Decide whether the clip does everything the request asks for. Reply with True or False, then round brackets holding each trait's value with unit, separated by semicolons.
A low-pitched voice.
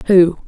False (185 Hz)